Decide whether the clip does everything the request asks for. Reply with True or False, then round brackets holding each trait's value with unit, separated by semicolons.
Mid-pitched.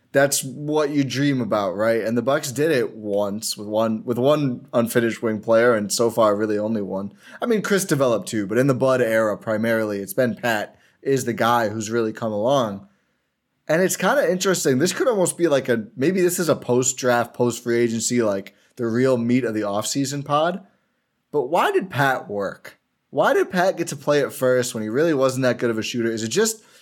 False (120 Hz)